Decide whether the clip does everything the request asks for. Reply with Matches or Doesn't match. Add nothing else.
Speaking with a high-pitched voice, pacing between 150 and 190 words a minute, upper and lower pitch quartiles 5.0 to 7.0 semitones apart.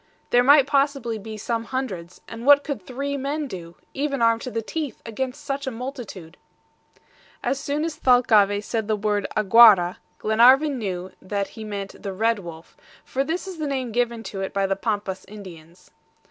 Matches